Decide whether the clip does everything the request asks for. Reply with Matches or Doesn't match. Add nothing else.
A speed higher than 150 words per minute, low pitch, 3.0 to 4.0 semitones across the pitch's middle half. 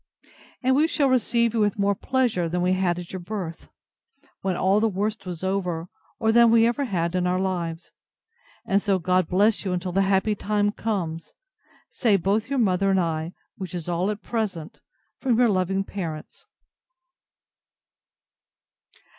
Doesn't match